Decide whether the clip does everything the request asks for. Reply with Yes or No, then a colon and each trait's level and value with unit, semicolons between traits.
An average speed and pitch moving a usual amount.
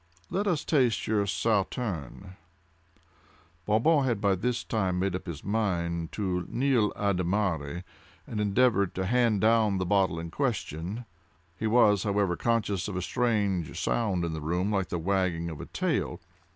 Yes: average, 165 wpm; average, 4.0 semitones